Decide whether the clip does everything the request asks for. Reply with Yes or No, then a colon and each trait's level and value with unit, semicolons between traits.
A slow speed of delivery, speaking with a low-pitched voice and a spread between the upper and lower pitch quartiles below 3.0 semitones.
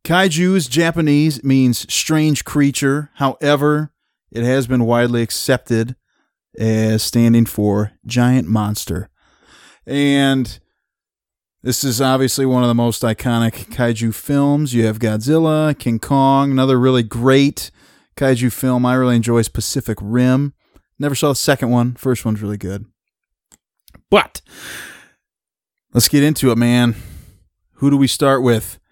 No: slow, 130 wpm; low, 125 Hz; average, 3.3 semitones